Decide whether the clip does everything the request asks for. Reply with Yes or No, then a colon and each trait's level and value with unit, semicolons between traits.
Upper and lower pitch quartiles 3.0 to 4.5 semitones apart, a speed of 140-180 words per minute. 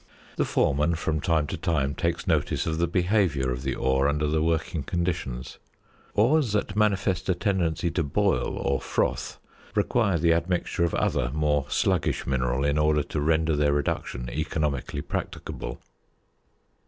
Yes: average, 3.4 semitones; average, 155 wpm